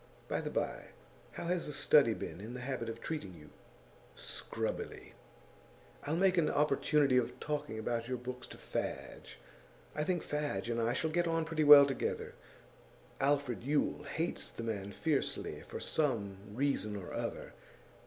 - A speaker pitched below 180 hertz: Yes, medium, 140 Hz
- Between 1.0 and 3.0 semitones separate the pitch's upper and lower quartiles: No, average, 4.7 semitones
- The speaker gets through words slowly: No, average, 160 wpm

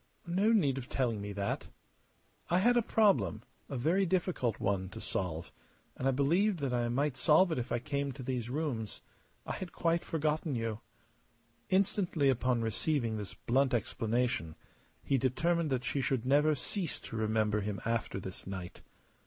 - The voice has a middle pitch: No, low, 130 Hz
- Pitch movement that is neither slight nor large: No, wide, 5.9 semitones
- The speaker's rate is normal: Yes, average, 170 wpm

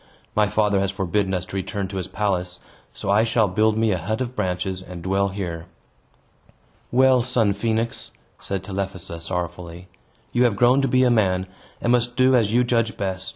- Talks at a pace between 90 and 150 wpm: No, average, 190 wpm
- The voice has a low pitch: Yes, low, 100 Hz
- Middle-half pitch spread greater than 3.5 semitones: Yes, average, 3.9 semitones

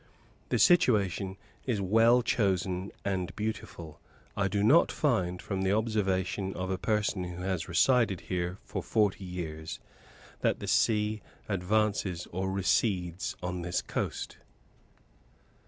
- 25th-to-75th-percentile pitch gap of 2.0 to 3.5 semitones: Yes, average, 2.9 semitones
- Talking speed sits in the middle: No, slow, 125 wpm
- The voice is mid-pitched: No, very low, 95 Hz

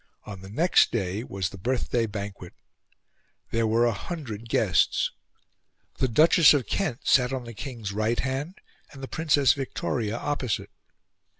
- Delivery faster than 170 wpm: No, average, 145 wpm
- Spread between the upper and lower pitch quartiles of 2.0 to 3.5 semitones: No, average, 4.3 semitones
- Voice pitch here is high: No, low, 120 Hz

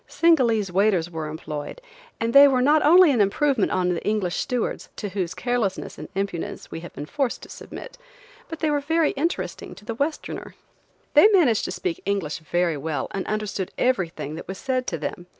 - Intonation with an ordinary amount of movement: No, wide, 7.9 semitones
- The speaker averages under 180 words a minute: No, average, 185 wpm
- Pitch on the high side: Yes, high, 210 Hz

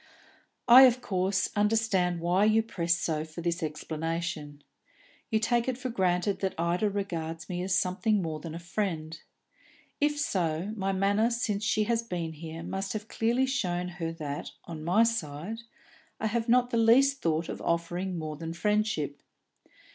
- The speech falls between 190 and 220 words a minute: No, average, 165 wpm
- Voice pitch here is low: No, medium, 185 Hz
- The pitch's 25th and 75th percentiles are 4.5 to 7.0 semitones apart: Yes, average, 4.9 semitones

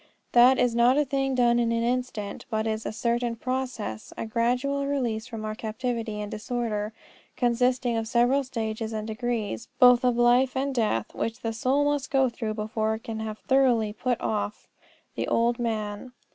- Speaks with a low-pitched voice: No, high, 235 Hz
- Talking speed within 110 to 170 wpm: No, average, 180 wpm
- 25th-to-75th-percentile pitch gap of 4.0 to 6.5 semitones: No, narrow, 2.5 semitones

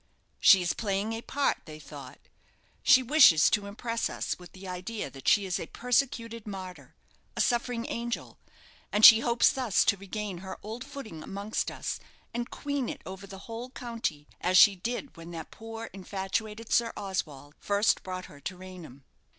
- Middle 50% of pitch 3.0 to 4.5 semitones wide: Yes, average, 4.1 semitones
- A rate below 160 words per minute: No, average, 175 wpm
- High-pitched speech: Yes, high, 205 Hz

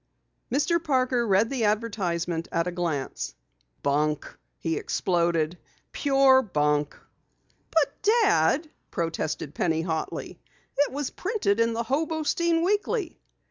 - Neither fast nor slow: No, slow, 110 wpm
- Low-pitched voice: No, high, 225 Hz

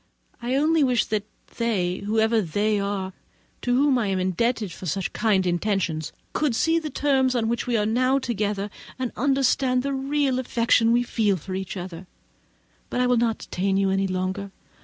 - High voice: Yes, high, 225 Hz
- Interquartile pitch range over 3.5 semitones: Yes, average, 4.6 semitones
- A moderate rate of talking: Yes, average, 180 wpm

